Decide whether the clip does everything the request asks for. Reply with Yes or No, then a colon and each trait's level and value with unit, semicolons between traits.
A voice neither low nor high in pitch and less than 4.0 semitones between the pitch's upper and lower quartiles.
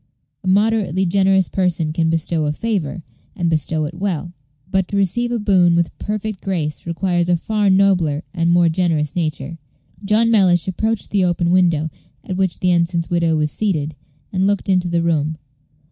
Yes: medium, 175 Hz; average, 2.9 semitones